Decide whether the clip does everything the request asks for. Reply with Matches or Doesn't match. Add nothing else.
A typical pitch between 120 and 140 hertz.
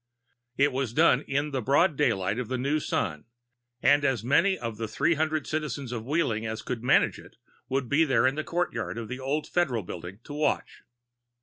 Matches